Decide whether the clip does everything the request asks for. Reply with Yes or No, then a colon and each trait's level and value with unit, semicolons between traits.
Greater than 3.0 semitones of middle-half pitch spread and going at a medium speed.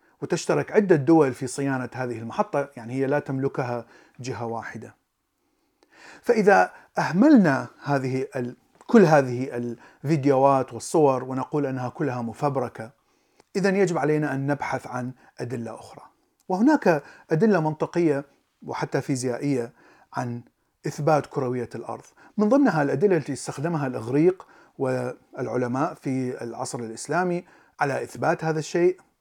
Yes: average, 4.5 semitones; average, 115 wpm